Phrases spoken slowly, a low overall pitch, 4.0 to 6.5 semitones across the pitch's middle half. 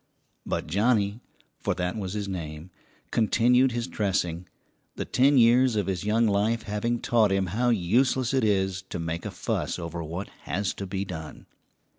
No: average, 175 wpm; low, 100 Hz; average, 4.3 semitones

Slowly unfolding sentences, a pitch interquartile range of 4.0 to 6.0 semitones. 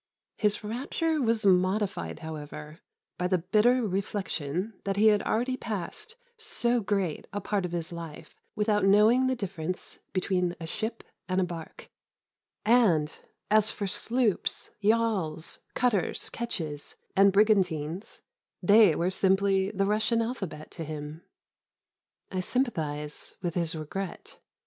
Yes: slow, 130 wpm; average, 4.5 semitones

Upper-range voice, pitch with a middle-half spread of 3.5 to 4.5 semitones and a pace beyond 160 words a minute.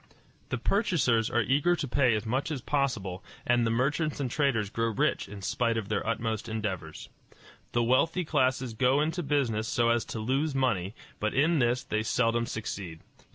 No: low, 120 Hz; average, 4.0 semitones; average, 180 wpm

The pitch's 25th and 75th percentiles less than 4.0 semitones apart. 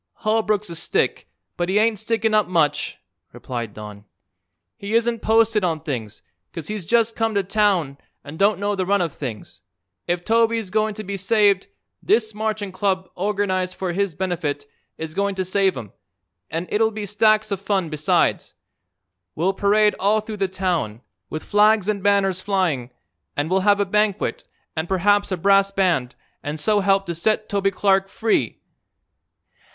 Yes: average, 3.4 semitones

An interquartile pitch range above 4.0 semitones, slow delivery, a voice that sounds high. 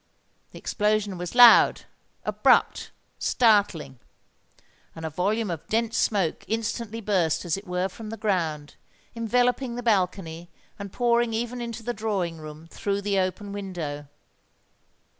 Yes: average, 4.5 semitones; slow, 125 wpm; high, 205 Hz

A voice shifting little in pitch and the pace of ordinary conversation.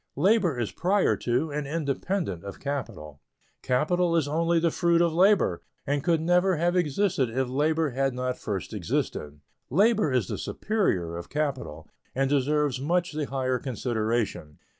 No: wide, 5.5 semitones; average, 155 wpm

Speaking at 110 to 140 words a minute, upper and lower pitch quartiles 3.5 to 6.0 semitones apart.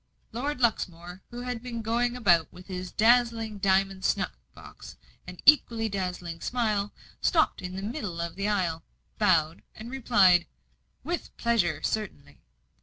Yes: slow, 135 wpm; average, 4.5 semitones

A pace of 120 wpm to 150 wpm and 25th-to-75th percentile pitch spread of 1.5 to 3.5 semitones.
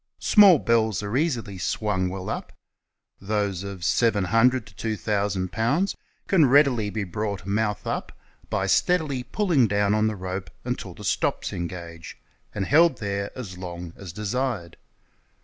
No: average, 145 wpm; average, 4.7 semitones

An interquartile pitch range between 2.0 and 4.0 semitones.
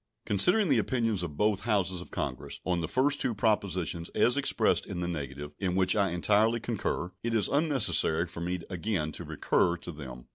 No: average, 4.8 semitones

